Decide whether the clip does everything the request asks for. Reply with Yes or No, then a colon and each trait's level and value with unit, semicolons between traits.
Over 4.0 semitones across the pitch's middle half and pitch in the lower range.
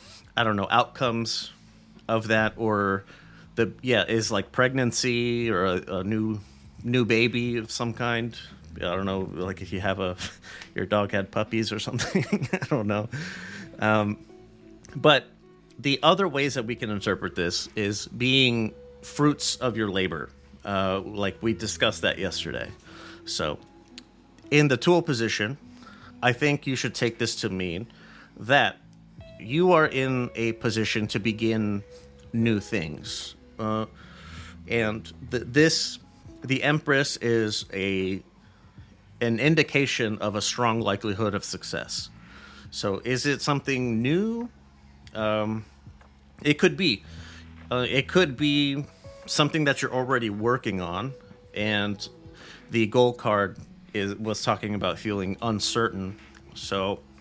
Yes: average, 4.4 semitones; low, 110 Hz